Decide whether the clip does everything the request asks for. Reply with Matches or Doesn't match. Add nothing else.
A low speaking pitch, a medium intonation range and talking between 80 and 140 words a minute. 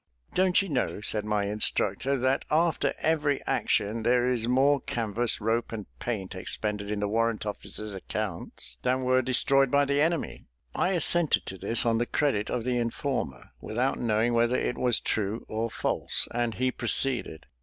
Doesn't match